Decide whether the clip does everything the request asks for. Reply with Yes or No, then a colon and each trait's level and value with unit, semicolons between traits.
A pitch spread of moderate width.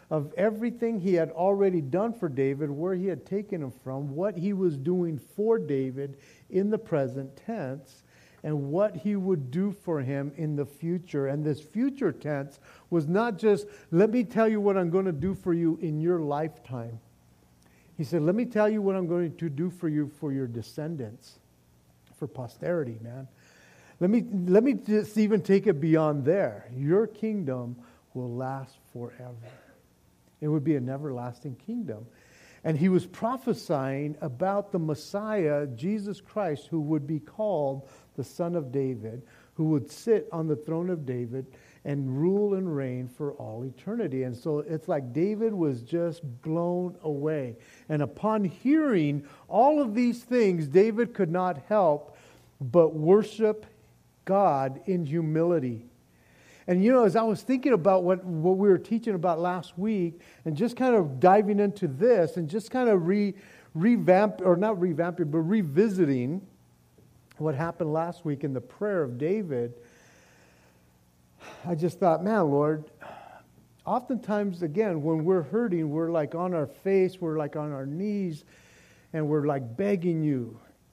No: wide, 6.1 semitones